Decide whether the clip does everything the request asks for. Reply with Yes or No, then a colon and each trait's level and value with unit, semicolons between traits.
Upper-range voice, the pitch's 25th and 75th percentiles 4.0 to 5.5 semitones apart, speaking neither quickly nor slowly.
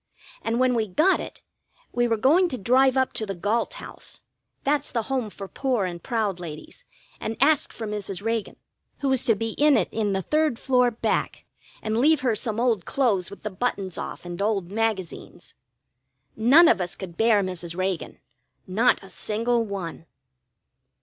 Yes: high, 225 Hz; average, 4.5 semitones; average, 180 wpm